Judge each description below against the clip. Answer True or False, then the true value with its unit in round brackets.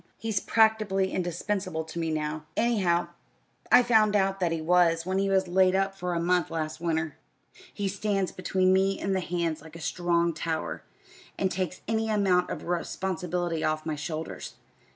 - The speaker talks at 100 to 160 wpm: False (170 wpm)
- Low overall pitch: False (180 Hz)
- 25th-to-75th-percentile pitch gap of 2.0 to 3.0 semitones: True (2.7 semitones)